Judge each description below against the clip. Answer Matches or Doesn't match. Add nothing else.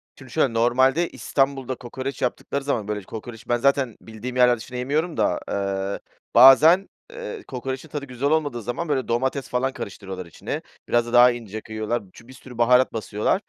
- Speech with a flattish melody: Doesn't match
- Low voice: Matches